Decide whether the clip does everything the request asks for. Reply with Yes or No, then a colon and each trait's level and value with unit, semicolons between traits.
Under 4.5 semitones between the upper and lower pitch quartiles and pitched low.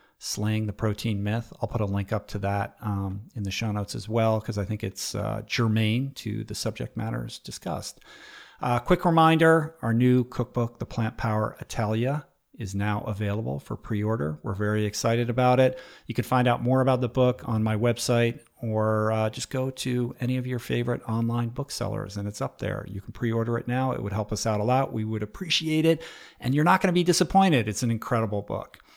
Yes: average, 3.0 semitones; low, 115 Hz